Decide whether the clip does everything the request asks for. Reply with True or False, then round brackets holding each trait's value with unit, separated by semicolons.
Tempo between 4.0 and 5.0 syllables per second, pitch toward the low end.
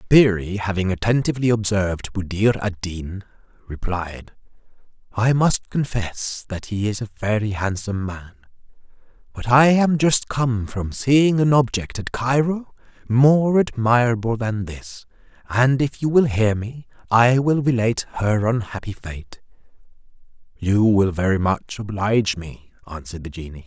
True (4.5 syllables/s; 110 Hz)